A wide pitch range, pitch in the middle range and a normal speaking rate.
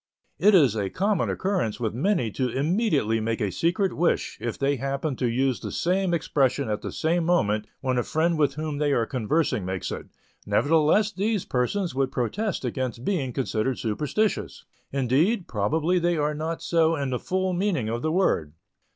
Yes: wide, 6.0 semitones; medium, 145 Hz; average, 180 wpm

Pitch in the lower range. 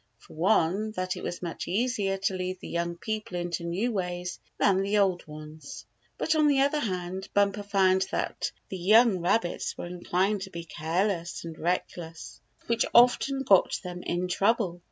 No: medium, 185 Hz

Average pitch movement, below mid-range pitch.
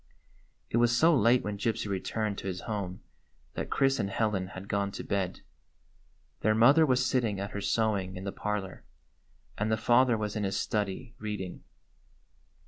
Yes: average, 3.0 semitones; low, 105 Hz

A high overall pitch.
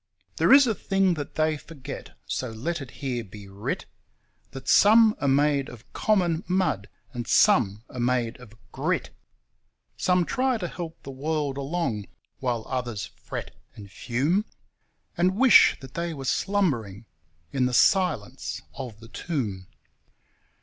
No: low, 135 Hz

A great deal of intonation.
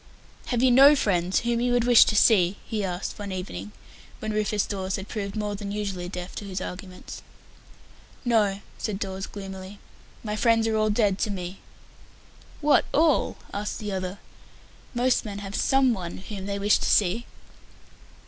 No: average, 2.8 semitones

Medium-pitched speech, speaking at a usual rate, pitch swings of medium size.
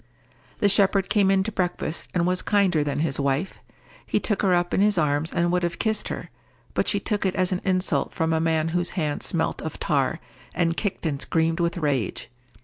No: medium, 175 Hz; fast, 215 wpm; average, 3.0 semitones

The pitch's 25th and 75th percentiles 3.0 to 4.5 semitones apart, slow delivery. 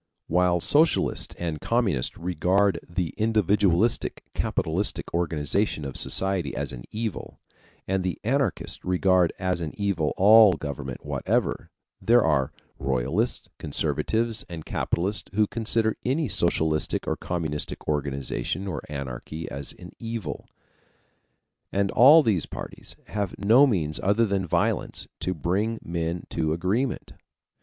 No: average, 5.3 semitones; slow, 125 wpm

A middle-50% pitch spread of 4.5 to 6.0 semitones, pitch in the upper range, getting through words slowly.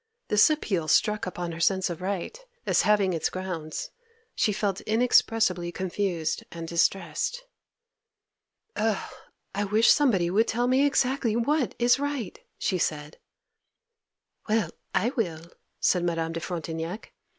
Yes: average, 4.9 semitones; high, 195 Hz; slow, 130 wpm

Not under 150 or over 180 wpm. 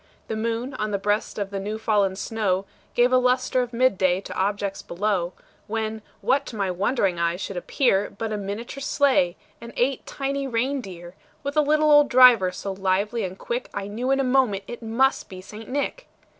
No: average, 200 wpm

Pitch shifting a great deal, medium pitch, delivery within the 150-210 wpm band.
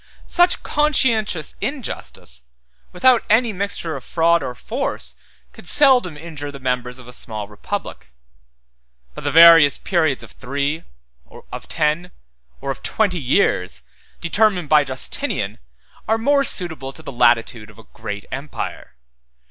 No: wide, 7.9 semitones; medium, 155 Hz; average, 140 wpm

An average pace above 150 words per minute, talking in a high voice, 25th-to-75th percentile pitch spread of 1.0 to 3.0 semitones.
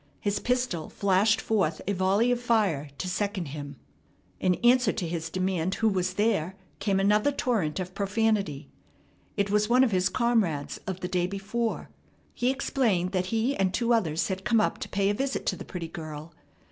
No: average, 185 wpm; high, 195 Hz; average, 3.8 semitones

